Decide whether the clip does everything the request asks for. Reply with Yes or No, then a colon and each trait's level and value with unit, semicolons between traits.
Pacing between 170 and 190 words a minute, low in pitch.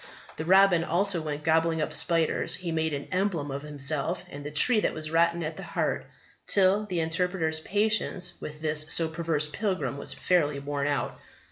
No: average, 180 wpm; medium, 160 Hz